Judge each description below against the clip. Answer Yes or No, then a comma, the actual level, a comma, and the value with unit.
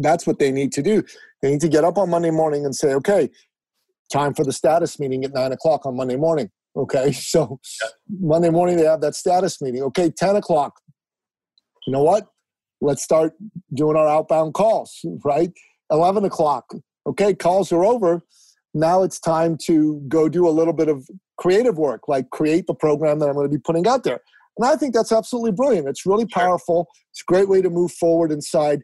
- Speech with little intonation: No, average, 3.6 semitones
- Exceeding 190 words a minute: Yes, average, 200 wpm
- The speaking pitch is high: No, medium, 165 Hz